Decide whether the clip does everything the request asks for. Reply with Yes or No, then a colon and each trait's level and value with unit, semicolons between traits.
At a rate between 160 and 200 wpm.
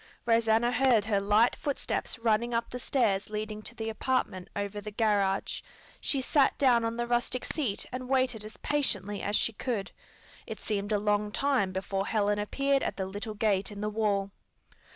Yes: average, 180 wpm